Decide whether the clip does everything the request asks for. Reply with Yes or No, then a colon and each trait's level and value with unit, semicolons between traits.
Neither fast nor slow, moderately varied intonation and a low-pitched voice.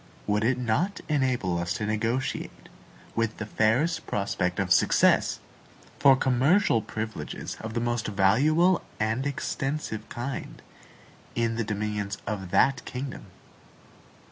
No: slow, 120 wpm; average, 4.0 semitones; low, 115 Hz